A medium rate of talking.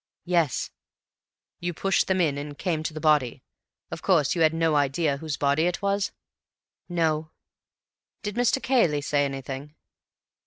Yes: average, 150 wpm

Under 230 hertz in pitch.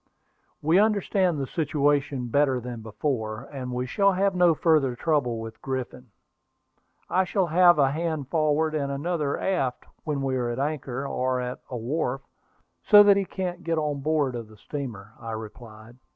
Yes: medium, 140 Hz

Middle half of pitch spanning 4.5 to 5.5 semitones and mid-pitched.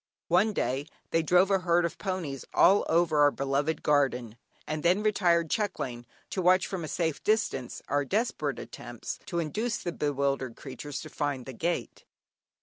Yes: average, 5.0 semitones; medium, 160 Hz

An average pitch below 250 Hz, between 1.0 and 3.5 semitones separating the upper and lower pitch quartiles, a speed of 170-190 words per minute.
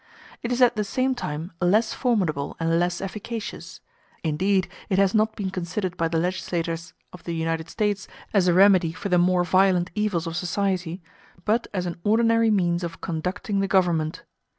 Yes: medium, 185 Hz; average, 3.2 semitones; average, 175 wpm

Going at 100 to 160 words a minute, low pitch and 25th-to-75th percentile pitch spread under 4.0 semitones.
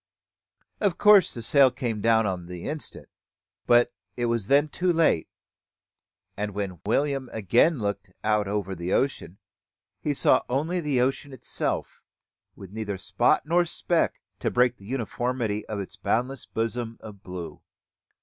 No: average, 150 wpm; low, 115 Hz; average, 5.2 semitones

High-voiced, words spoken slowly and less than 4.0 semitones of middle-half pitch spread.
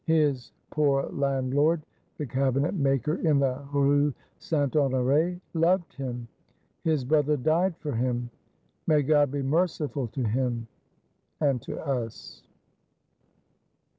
No: medium, 140 Hz; slow, 115 wpm; average, 3.0 semitones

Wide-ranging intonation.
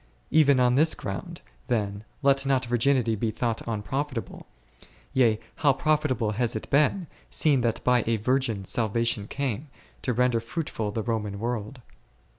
No: average, 3.7 semitones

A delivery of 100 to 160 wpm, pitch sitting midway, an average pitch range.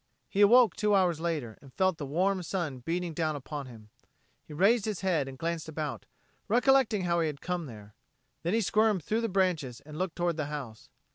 No: fast, 205 wpm; medium, 170 Hz; average, 4.8 semitones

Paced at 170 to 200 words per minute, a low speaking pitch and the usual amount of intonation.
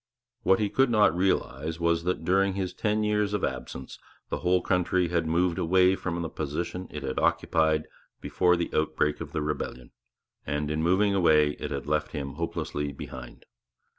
Yes: average, 175 wpm; very low, 85 Hz; average, 3.6 semitones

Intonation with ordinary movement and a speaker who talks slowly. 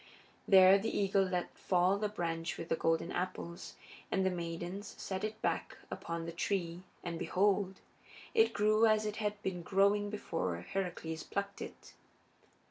No: average, 3.2 semitones; average, 155 wpm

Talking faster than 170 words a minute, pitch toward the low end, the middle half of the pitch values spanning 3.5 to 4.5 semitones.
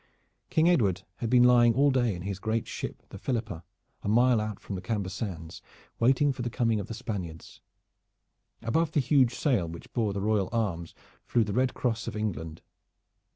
Yes: average, 190 wpm; low, 110 Hz; average, 4.1 semitones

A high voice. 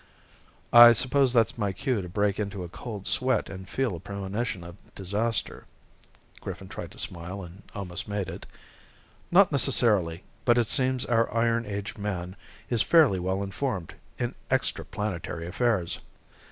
No: low, 100 Hz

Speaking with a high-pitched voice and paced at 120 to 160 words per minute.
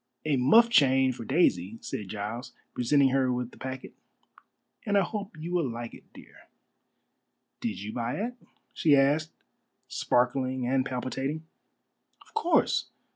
No: low, 130 Hz; average, 140 wpm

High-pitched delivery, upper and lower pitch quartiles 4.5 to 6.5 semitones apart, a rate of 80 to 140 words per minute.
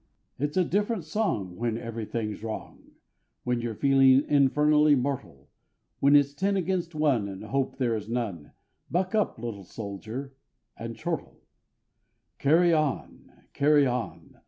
No: low, 135 Hz; average, 5.1 semitones; slow, 135 wpm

